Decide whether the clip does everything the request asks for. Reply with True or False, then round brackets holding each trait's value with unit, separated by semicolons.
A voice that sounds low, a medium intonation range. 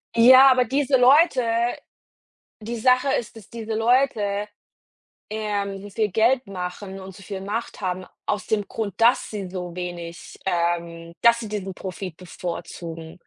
False (205 Hz; 4.3 semitones)